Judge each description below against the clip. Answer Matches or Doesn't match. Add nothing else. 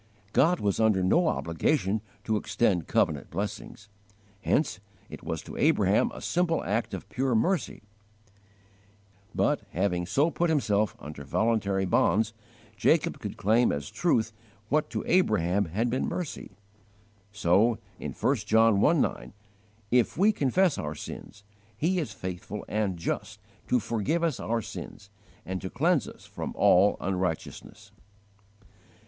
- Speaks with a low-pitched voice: Matches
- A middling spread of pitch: Doesn't match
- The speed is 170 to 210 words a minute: Doesn't match